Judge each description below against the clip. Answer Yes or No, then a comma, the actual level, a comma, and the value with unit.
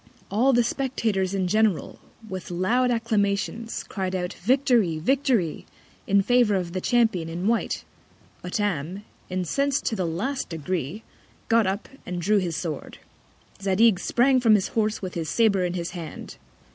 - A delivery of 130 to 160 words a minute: Yes, average, 150 wpm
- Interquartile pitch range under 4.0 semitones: No, average, 4.4 semitones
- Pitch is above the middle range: Yes, high, 200 Hz